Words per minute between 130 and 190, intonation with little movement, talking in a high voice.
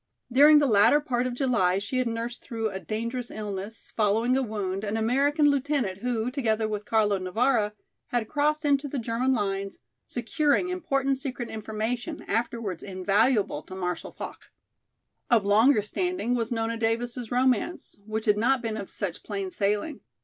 No: average, 160 wpm; average, 3.9 semitones; high, 230 Hz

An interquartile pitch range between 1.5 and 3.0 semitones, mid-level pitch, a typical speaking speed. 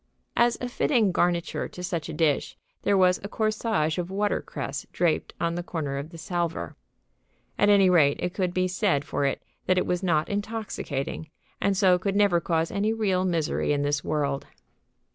No: average, 3.9 semitones; medium, 180 Hz; average, 180 wpm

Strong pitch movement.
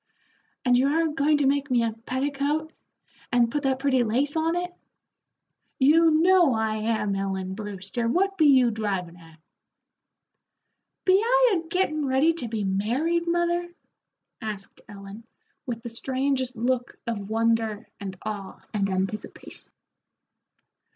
Yes: wide, 6.3 semitones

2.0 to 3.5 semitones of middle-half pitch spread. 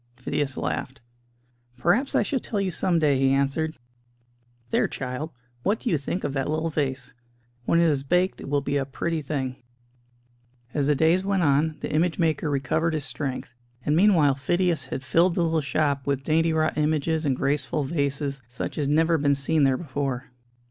Yes: average, 3.1 semitones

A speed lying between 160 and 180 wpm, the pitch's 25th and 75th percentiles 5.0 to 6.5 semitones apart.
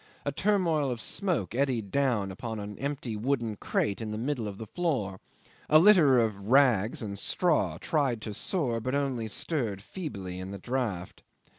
Yes: average, 170 wpm; wide, 5.5 semitones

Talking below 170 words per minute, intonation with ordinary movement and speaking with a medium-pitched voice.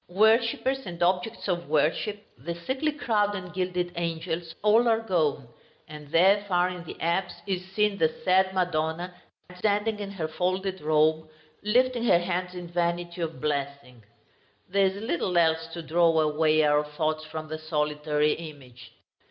Yes: average, 155 wpm; average, 3.6 semitones; medium, 175 Hz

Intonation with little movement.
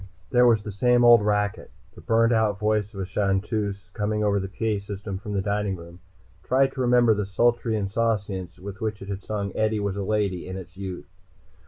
Yes: narrow, 2.2 semitones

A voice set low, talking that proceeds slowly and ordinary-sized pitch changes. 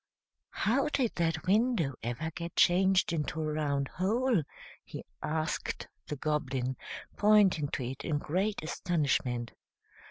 No: medium, 160 Hz; slow, 125 wpm; average, 4.9 semitones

